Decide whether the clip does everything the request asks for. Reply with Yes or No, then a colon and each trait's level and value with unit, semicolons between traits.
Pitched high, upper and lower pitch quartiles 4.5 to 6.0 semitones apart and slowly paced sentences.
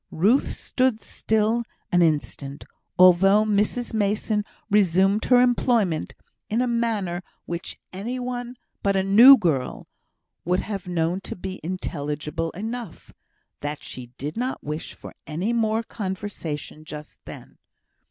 Yes: high, 195 Hz; average, 5.2 semitones; slow, 130 wpm